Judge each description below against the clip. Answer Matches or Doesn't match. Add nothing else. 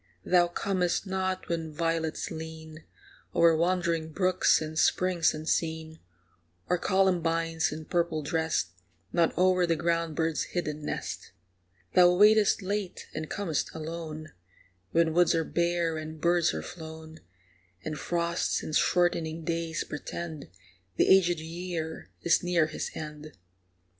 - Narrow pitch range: Matches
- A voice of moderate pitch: Matches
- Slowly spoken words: Matches